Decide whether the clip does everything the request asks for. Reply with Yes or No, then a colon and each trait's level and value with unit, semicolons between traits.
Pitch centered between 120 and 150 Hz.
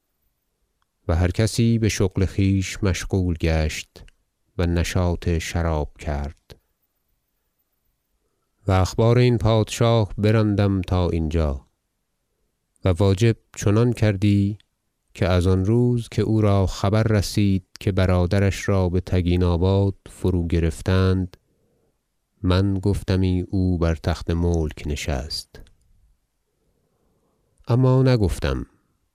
No: very low, 95 Hz